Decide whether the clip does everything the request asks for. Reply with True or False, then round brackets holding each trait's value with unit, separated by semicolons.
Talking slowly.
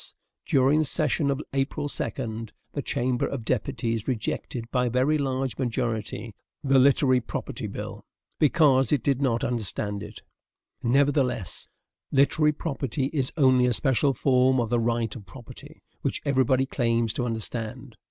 False (145 wpm)